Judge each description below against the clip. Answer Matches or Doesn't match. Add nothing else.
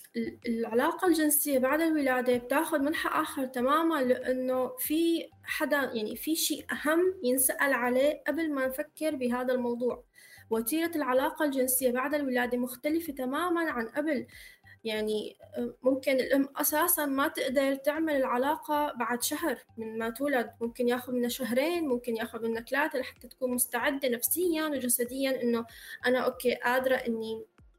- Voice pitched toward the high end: Matches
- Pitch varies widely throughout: Doesn't match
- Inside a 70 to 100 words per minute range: Doesn't match